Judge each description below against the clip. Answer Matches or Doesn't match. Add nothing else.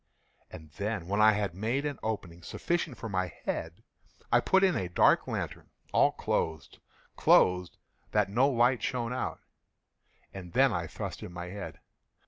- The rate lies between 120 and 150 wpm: Doesn't match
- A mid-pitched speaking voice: Doesn't match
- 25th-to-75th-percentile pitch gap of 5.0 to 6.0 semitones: Matches